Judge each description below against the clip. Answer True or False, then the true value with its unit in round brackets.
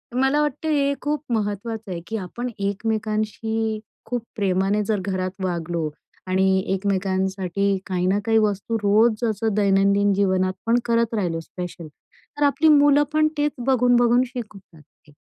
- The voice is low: False (205 Hz)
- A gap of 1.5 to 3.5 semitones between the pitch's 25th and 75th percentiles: False (3.9 semitones)